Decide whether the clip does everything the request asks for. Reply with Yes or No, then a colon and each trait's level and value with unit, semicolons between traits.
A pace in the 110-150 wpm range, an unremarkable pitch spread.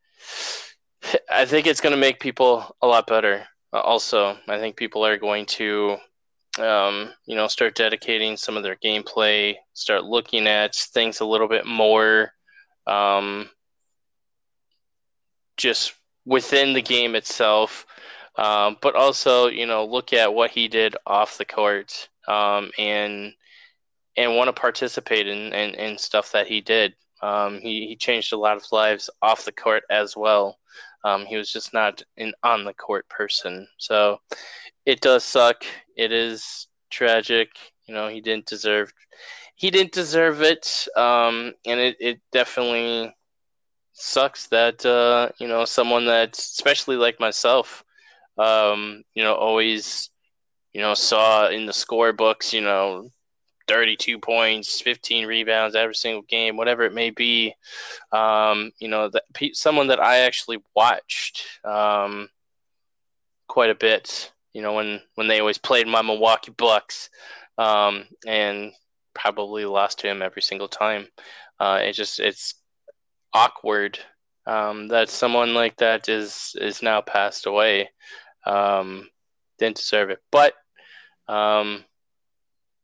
No: average, 145 wpm; narrow, 2.0 semitones